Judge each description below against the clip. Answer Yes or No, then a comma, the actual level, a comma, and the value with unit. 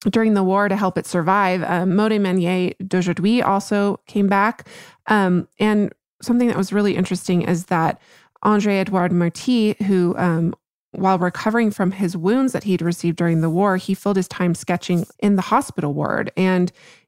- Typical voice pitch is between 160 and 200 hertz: Yes, high, 190 Hz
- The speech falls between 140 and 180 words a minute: Yes, average, 170 wpm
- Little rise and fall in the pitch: Yes, narrow, 2.3 semitones